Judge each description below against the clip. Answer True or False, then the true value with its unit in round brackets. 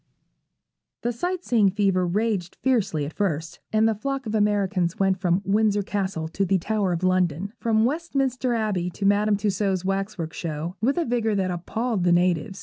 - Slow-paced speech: False (175 wpm)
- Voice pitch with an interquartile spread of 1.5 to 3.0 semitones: False (3.5 semitones)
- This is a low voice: False (200 Hz)